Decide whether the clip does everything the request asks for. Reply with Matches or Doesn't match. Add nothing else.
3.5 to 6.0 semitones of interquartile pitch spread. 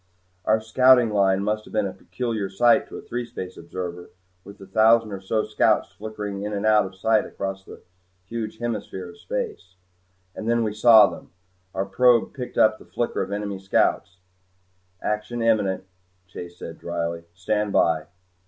Doesn't match